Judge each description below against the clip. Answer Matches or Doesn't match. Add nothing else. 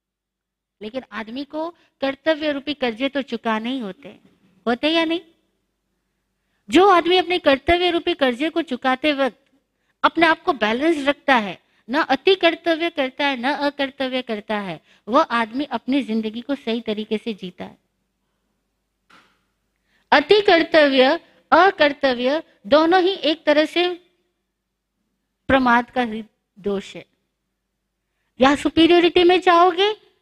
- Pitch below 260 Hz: Doesn't match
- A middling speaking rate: Matches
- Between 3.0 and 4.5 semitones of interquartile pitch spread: Doesn't match